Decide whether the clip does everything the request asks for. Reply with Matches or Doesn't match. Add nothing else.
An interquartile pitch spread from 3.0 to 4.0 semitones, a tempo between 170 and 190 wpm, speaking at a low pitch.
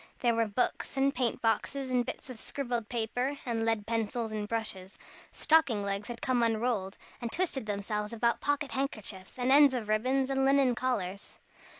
Doesn't match